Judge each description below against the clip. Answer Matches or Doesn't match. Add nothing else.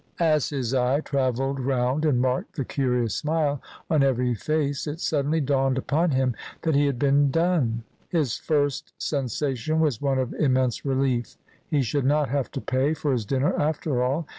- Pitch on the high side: Doesn't match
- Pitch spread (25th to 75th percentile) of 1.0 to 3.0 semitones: Matches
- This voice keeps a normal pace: Matches